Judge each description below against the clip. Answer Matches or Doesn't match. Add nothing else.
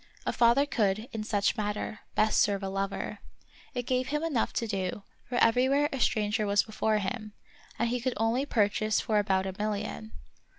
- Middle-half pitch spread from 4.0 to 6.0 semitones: Doesn't match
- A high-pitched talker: Matches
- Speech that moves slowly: Doesn't match